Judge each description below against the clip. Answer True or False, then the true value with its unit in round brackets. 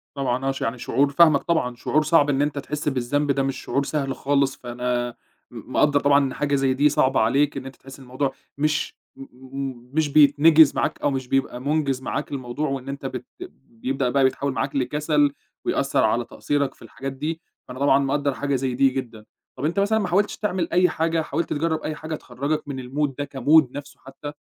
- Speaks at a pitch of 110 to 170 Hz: True (140 Hz)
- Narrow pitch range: True (2.2 semitones)